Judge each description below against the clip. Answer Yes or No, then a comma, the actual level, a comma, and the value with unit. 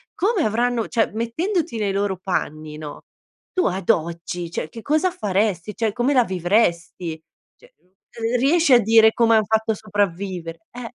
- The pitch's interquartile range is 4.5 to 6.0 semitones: Yes, average, 5.1 semitones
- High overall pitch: Yes, high, 215 Hz